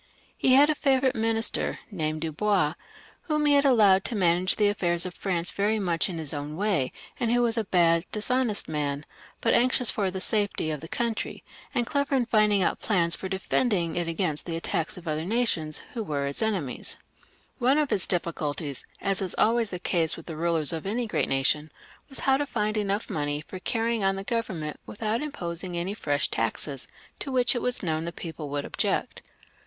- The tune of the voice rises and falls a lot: Yes, wide, 5.9 semitones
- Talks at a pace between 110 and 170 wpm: No, fast, 205 wpm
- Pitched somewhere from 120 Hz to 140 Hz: No, high, 190 Hz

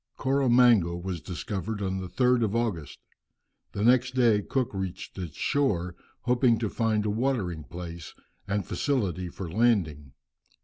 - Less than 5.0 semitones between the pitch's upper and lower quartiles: No, wide, 5.5 semitones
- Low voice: Yes, low, 105 Hz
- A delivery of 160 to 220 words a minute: No, average, 140 wpm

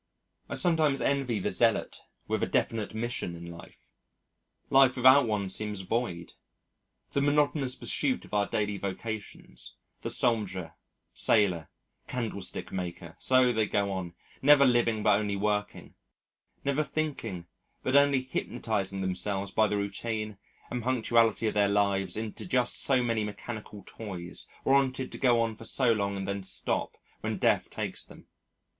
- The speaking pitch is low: Yes, low, 110 Hz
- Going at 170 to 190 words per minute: No, average, 145 wpm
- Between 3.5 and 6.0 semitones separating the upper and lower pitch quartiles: Yes, average, 4.2 semitones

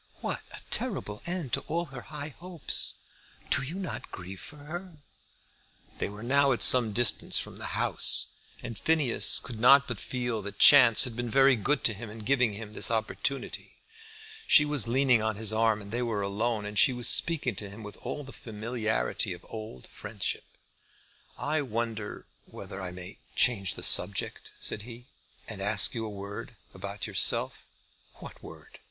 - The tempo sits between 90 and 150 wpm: No, average, 175 wpm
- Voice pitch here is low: Yes, low, 115 Hz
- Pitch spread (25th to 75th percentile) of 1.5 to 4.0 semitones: No, average, 4.5 semitones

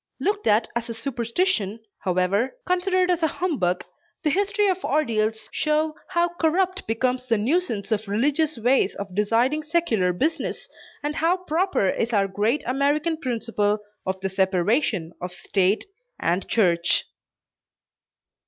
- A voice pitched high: Yes, high, 240 Hz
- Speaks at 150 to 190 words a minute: No, slow, 135 wpm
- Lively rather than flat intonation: Yes, wide, 7.8 semitones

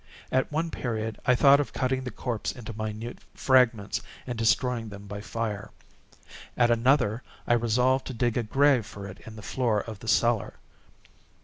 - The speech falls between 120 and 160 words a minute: No, average, 175 wpm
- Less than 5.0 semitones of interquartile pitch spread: Yes, average, 2.8 semitones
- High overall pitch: No, low, 115 Hz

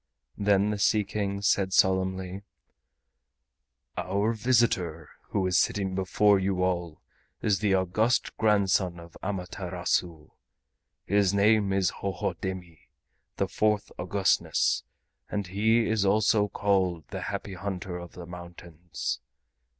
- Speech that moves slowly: Yes, slow, 115 wpm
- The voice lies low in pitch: Yes, very low, 95 Hz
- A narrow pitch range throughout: Yes, narrow, 2.3 semitones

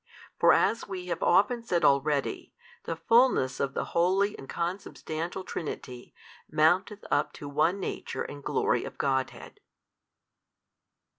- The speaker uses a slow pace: Yes, slow, 130 wpm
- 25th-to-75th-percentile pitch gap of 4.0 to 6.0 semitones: Yes, average, 5.2 semitones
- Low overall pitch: No, medium, 170 Hz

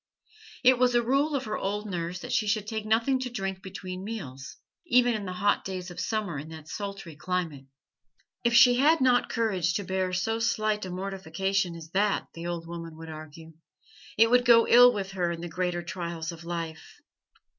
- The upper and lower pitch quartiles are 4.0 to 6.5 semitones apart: Yes, average, 4.7 semitones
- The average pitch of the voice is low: No, high, 190 Hz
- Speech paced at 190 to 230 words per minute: Yes, average, 200 wpm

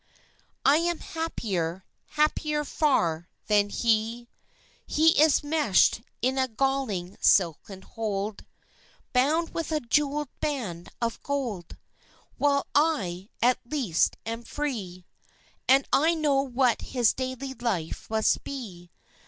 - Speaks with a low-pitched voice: No, very high, 250 Hz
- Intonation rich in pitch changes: Yes, wide, 6.3 semitones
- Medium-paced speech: No, slow, 115 wpm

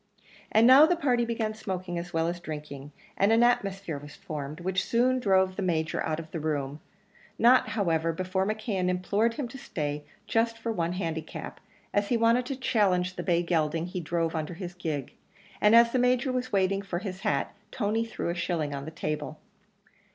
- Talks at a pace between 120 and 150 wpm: No, average, 195 wpm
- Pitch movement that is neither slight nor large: No, wide, 5.7 semitones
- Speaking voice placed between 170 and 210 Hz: Yes, medium, 185 Hz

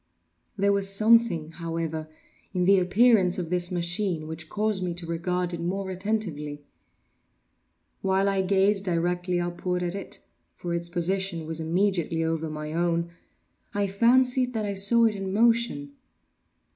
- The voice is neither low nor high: Yes, medium, 180 Hz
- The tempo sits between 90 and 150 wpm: Yes, average, 145 wpm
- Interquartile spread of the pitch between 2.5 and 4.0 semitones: Yes, average, 3.0 semitones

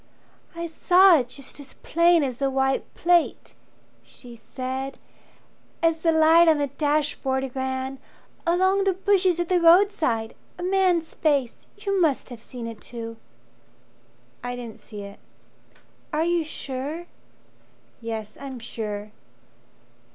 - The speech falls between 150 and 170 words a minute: No, slow, 135 wpm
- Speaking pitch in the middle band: No, very high, 285 Hz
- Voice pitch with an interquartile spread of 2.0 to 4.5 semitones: No, wide, 5.4 semitones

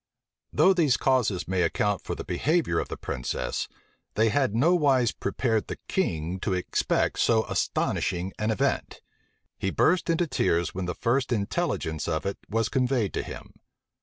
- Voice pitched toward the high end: No, low, 110 Hz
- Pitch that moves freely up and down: Yes, wide, 6.4 semitones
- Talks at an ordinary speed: Yes, average, 160 wpm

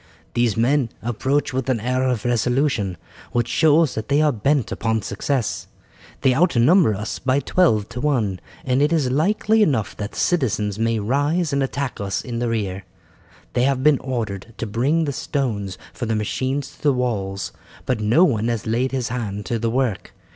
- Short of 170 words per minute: No, average, 185 wpm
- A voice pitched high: No, low, 125 Hz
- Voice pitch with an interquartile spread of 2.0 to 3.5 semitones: No, average, 4.2 semitones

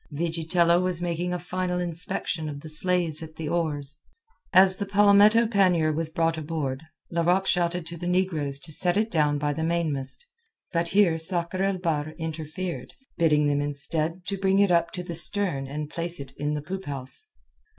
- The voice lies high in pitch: No, medium, 170 Hz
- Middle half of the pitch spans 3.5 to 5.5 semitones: No, average, 3.0 semitones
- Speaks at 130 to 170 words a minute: No, average, 180 wpm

